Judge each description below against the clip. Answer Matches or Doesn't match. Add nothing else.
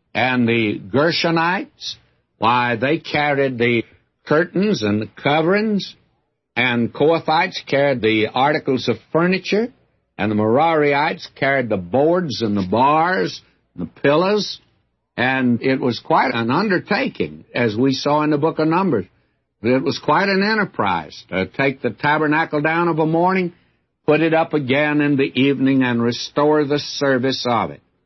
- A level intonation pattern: Doesn't match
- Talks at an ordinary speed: Matches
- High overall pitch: Doesn't match